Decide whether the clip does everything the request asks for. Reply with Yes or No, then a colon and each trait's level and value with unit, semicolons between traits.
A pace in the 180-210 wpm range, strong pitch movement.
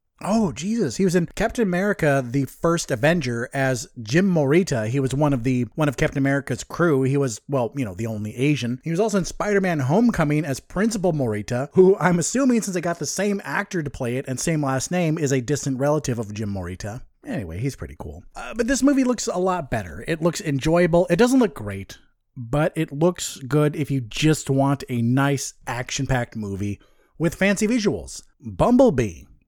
Yes: average, 200 wpm; wide, 5.7 semitones